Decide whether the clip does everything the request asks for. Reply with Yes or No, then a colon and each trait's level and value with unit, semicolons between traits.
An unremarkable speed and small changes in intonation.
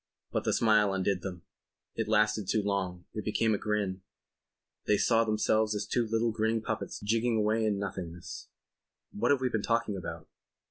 Yes: average, 175 wpm; narrow, 2.0 semitones